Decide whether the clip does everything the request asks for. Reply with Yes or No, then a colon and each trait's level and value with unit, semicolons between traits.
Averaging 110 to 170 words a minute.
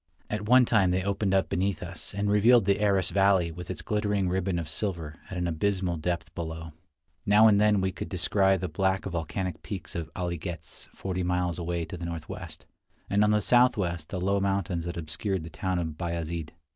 No: average, 200 wpm